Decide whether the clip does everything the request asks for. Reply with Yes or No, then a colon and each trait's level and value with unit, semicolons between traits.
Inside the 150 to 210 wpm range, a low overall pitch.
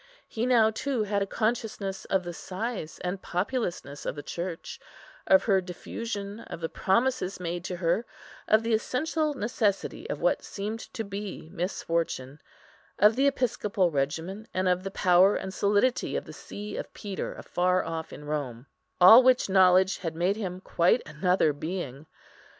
No: average, 160 wpm; high, 190 Hz